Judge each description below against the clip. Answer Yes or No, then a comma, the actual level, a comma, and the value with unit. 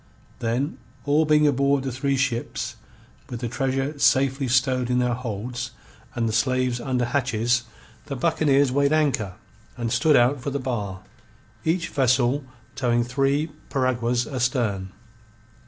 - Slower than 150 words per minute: Yes, average, 140 wpm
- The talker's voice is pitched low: Yes, low, 130 Hz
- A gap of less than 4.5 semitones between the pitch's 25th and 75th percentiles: Yes, narrow, 2.6 semitones